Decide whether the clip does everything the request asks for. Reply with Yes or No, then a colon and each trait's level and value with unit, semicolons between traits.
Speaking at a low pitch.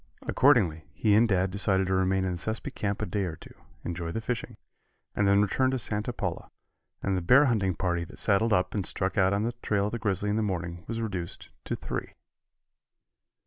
Yes: low, 100 Hz